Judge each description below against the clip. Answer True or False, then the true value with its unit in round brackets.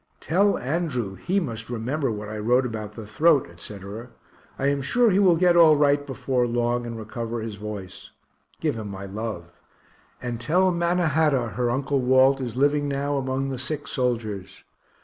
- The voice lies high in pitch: False (125 Hz)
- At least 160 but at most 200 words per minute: True (170 wpm)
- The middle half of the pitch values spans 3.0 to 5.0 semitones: True (4.7 semitones)